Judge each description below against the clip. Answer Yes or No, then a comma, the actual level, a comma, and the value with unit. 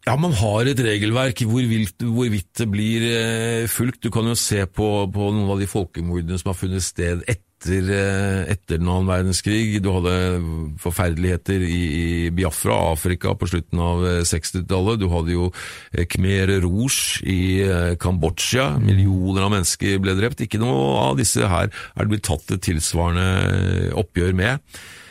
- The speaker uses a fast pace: No, average, 155 wpm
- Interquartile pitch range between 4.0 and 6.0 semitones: No, average, 3.3 semitones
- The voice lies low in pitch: Yes, very low, 95 Hz